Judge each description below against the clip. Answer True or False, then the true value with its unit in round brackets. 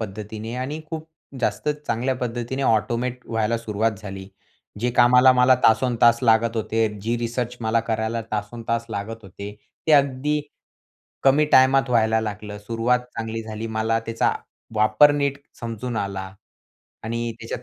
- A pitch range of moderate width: False (2.3 semitones)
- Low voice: True (115 Hz)